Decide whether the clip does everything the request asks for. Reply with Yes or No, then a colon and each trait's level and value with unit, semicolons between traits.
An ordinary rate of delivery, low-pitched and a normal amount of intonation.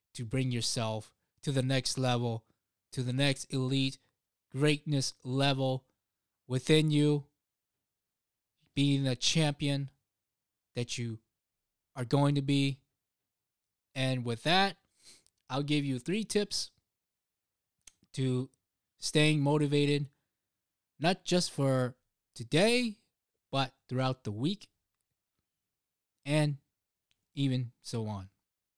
No: slow, 100 wpm; low, 130 Hz; average, 4.6 semitones